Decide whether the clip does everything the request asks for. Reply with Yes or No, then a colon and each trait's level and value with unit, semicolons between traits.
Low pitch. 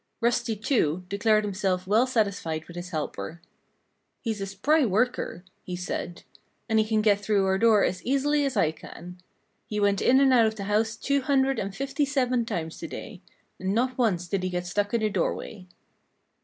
No: high, 210 Hz